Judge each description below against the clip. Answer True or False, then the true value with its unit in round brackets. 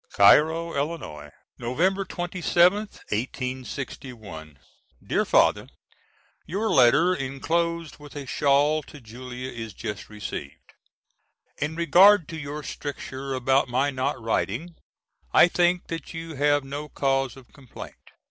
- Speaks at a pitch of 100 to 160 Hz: True (140 Hz)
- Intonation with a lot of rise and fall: False (4.8 semitones)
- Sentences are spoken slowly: True (120 wpm)